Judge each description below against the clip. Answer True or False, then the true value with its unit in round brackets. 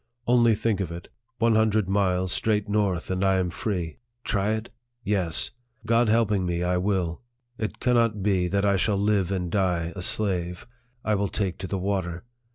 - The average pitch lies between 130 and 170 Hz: False (100 Hz)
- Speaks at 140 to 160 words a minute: False (180 wpm)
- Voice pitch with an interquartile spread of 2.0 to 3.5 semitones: True (2.9 semitones)